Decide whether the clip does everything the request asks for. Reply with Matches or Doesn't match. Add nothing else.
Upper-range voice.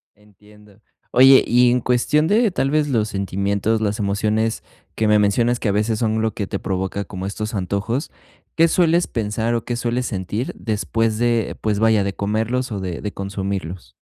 Doesn't match